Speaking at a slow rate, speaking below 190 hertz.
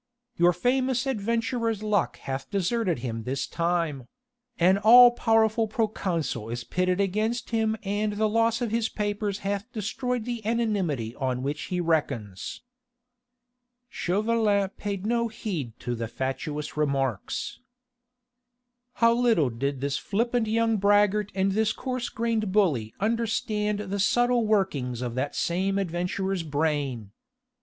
No: slow, 130 wpm; high, 200 Hz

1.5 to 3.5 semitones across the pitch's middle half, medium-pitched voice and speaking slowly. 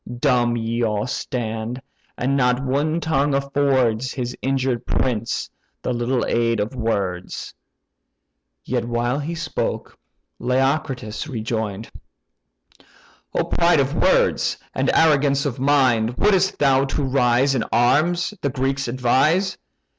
No: average, 2.9 semitones; low, 130 Hz; slow, 120 wpm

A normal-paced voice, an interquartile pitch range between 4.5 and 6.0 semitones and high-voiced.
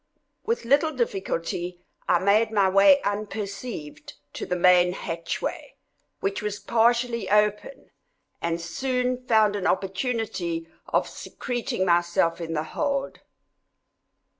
No: slow, 115 wpm; average, 5.3 semitones; high, 200 Hz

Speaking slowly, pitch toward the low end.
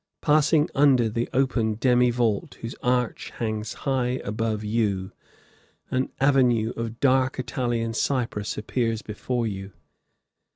Yes: slow, 120 wpm; low, 120 Hz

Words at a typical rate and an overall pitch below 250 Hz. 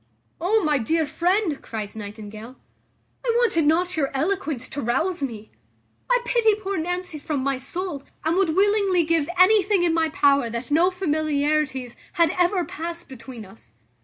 No: average, 160 wpm; very high, 320 Hz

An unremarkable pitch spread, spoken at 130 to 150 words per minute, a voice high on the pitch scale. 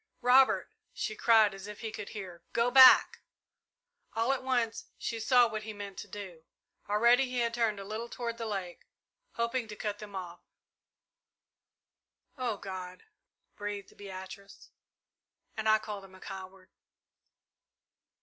Yes: average, 3.1 semitones; average, 145 wpm; high, 215 Hz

